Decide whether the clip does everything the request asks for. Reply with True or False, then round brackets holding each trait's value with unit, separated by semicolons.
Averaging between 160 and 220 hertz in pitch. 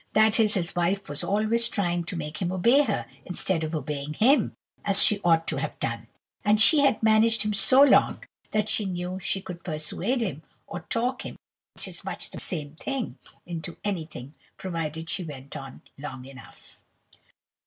True (185 Hz)